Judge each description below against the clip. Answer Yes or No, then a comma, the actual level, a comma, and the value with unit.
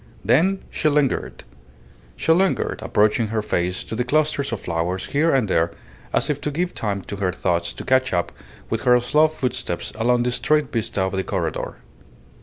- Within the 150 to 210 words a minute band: Yes, average, 185 wpm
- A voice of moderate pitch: No, low, 120 Hz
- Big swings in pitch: Yes, wide, 7.3 semitones